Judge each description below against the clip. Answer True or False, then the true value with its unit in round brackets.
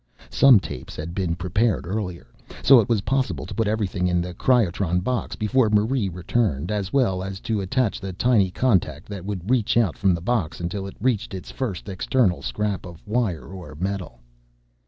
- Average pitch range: True (4.1 semitones)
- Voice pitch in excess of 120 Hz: False (100 Hz)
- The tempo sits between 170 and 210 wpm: True (185 wpm)